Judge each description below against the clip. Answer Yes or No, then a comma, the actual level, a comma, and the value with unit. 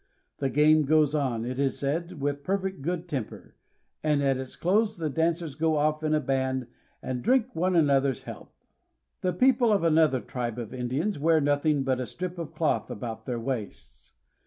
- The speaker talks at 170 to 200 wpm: Yes, average, 185 wpm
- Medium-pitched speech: Yes, medium, 150 Hz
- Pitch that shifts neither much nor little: Yes, average, 4.1 semitones